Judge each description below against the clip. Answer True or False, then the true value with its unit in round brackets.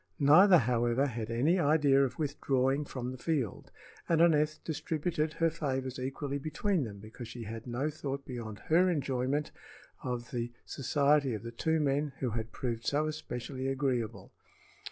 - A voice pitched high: False (135 Hz)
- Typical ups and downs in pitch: True (3.9 semitones)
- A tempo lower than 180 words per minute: True (155 wpm)